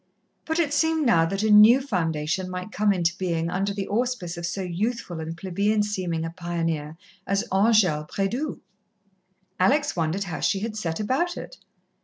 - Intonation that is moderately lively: Yes, average, 4.4 semitones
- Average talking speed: Yes, average, 170 wpm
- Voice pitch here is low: No, high, 195 Hz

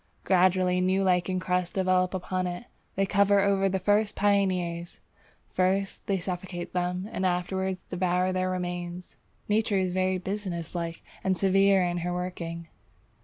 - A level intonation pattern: Yes, narrow, 1.4 semitones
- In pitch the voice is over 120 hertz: Yes, medium, 185 Hz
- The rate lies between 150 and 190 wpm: No, average, 140 wpm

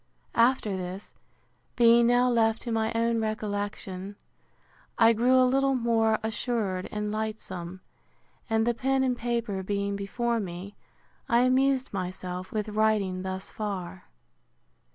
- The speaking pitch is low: No, high, 220 Hz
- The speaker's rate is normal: No, slow, 130 wpm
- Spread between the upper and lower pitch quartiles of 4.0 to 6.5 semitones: No, average, 3.2 semitones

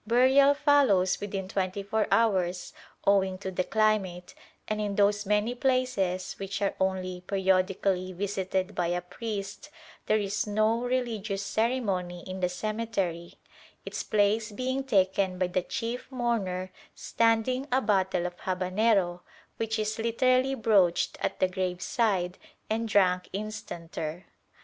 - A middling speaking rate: No, slow, 130 wpm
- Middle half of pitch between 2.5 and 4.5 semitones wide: Yes, average, 3.5 semitones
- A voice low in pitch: No, high, 200 Hz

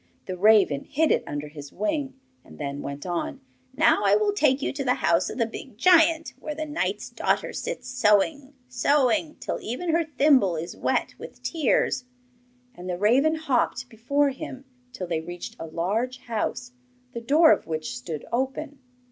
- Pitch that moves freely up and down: Yes, wide, 7.9 semitones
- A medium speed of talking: Yes, average, 175 wpm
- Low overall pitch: No, very high, 250 Hz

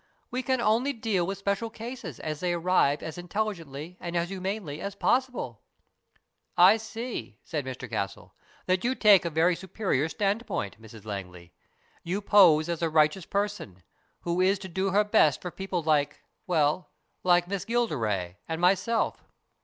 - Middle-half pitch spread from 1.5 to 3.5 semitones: No, average, 5.1 semitones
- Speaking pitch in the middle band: Yes, medium, 180 Hz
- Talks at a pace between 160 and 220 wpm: Yes, average, 165 wpm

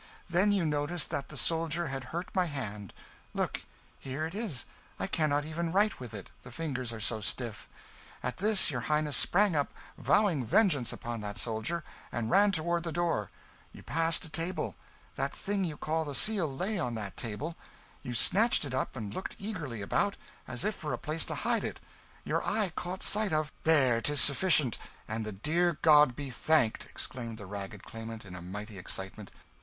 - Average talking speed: Yes, average, 190 wpm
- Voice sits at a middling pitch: Yes, medium, 150 Hz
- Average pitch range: No, wide, 6.7 semitones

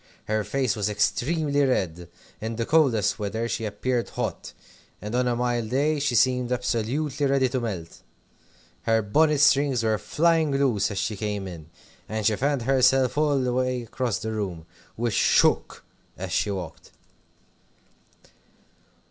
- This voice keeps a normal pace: Yes, average, 150 wpm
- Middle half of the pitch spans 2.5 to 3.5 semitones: No, average, 4.3 semitones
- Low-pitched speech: Yes, low, 120 Hz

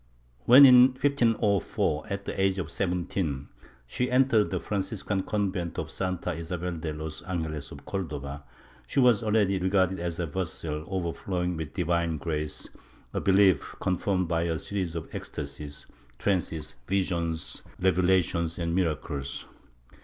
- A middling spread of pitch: Yes, average, 3.3 semitones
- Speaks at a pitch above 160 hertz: No, very low, 90 Hz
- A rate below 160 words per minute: Yes, average, 140 wpm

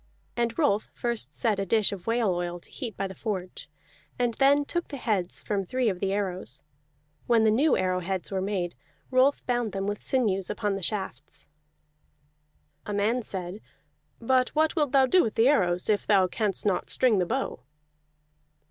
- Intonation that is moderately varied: Yes, average, 4.5 semitones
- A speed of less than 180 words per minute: No, average, 185 wpm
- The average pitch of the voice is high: Yes, high, 210 Hz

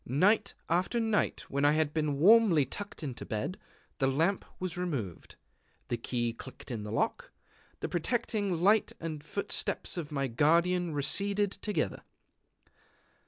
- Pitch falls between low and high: Yes, medium, 165 Hz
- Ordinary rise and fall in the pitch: No, wide, 6.2 semitones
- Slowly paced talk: No, average, 145 wpm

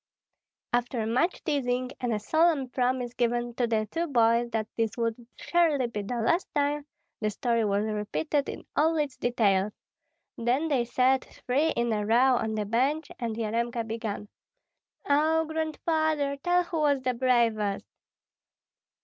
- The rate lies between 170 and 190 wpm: No, average, 150 wpm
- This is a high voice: Yes, high, 245 Hz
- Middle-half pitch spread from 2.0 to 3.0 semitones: No, average, 4.3 semitones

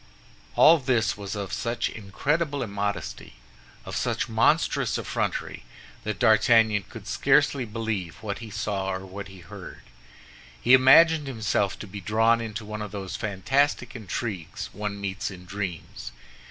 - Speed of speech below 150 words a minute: Yes, average, 140 wpm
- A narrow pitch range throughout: No, average, 3.0 semitones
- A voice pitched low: Yes, low, 105 Hz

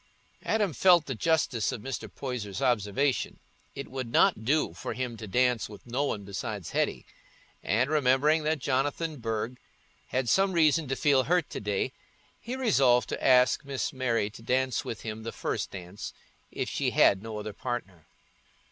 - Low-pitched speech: Yes, low, 125 Hz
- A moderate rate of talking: Yes, average, 170 wpm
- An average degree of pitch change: Yes, average, 4.7 semitones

